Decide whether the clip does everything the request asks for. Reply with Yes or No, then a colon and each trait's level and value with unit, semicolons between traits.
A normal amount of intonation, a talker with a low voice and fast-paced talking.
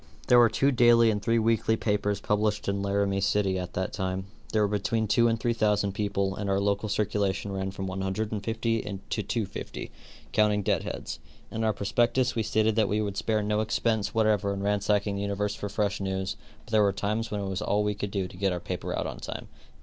No: narrow, 1.8 semitones; low, 105 Hz; fast, 220 wpm